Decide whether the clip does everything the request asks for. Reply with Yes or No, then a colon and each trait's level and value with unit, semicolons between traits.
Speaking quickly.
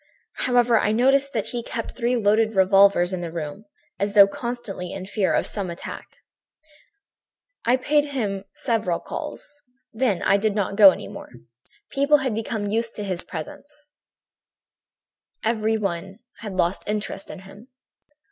No: average, 145 wpm